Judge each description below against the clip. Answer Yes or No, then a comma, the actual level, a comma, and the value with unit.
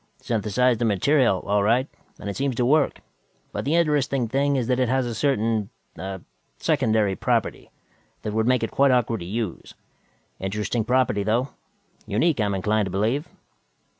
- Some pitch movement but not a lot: Yes, average, 4.0 semitones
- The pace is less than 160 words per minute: No, average, 170 wpm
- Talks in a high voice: No, low, 115 Hz